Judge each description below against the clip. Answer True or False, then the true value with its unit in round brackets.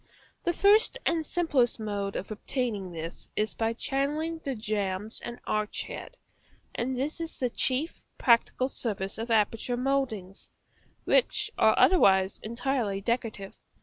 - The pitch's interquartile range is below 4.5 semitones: False (4.9 semitones)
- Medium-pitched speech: False (235 Hz)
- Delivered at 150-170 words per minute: False (135 wpm)